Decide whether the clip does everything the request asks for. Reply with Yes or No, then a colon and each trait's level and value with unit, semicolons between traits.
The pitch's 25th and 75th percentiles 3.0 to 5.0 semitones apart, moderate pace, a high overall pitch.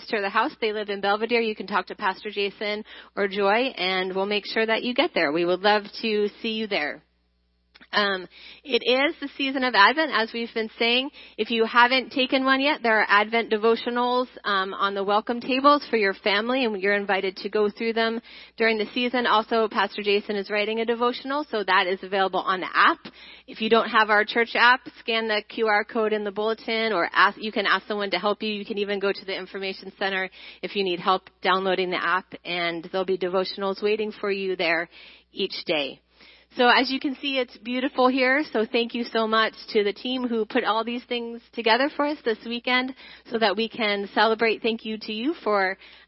No: average, 3.3 semitones; fast, 215 wpm; high, 220 Hz